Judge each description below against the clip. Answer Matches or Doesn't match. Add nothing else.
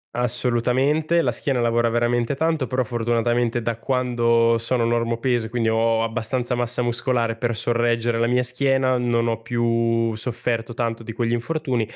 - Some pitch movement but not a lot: Doesn't match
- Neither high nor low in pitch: Doesn't match